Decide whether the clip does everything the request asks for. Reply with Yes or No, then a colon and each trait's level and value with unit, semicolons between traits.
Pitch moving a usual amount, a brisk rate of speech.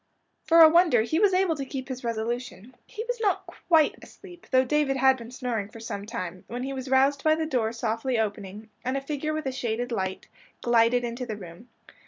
Yes: average, 4.7 semitones; fast, 215 wpm